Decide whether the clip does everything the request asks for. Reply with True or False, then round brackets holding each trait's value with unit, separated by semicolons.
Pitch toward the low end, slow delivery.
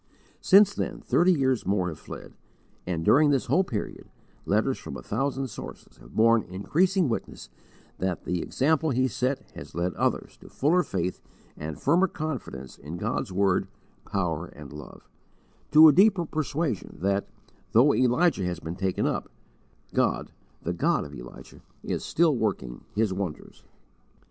False (115 Hz; 155 wpm)